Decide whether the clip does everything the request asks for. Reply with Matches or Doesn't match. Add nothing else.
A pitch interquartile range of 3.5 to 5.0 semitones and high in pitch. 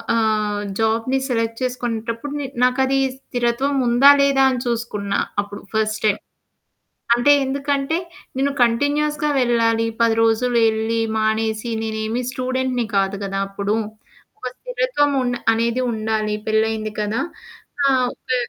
Doesn't match